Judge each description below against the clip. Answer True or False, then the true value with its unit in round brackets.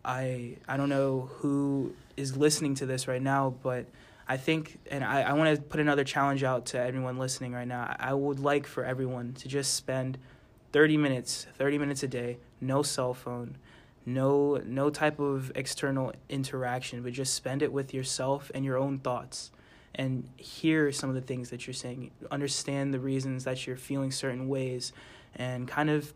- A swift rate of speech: False (185 wpm)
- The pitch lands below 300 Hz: True (135 Hz)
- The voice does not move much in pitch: True (1.8 semitones)